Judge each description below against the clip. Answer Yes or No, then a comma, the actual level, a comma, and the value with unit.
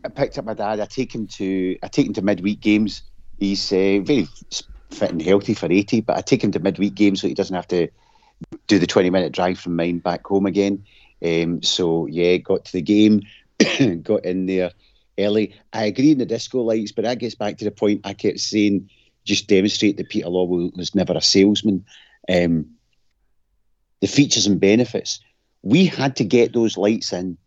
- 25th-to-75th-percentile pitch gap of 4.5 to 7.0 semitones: No, average, 2.9 semitones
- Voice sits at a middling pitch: No, low, 100 Hz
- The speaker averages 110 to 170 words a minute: No, average, 200 wpm